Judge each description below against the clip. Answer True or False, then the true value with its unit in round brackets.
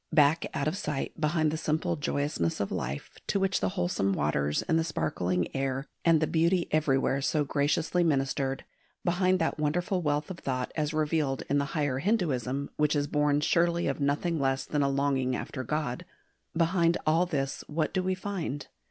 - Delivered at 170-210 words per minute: True (180 wpm)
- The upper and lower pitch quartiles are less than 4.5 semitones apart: True (3.6 semitones)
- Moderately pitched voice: True (150 Hz)